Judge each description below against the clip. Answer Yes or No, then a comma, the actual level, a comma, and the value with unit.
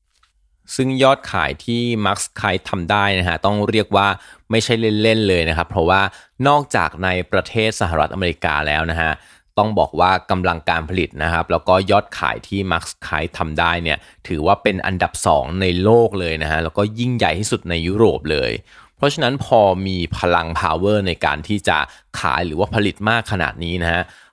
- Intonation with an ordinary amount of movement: Yes, average, 4.4 semitones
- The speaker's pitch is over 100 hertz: No, very low, 95 Hz